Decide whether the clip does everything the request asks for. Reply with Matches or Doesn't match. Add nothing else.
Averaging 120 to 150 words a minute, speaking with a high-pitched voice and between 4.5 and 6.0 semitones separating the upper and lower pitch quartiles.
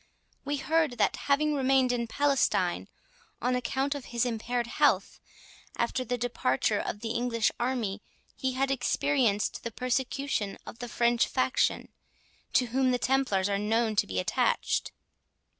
Doesn't match